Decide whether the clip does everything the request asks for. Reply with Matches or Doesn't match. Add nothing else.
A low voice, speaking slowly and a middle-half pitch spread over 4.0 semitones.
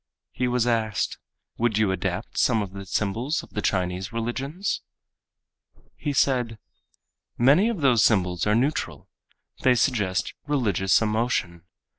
Matches